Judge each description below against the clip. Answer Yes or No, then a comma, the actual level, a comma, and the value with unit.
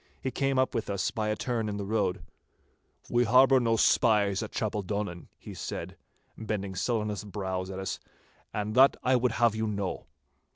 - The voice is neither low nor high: No, low, 105 Hz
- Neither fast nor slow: Yes, average, 175 wpm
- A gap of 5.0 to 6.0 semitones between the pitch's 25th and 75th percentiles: No, average, 2.9 semitones